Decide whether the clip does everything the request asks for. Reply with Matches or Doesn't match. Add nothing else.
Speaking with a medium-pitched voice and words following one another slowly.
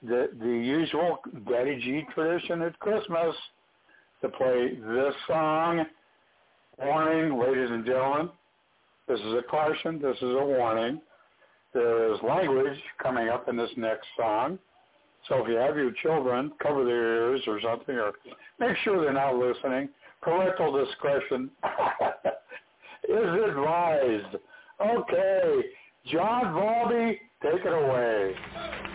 Matches